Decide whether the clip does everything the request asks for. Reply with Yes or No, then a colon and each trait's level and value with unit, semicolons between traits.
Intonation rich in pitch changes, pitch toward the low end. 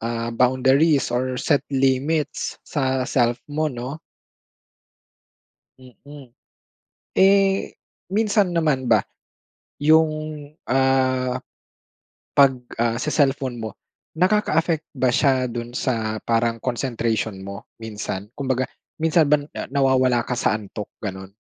No: average, 4.2 semitones; low, 130 Hz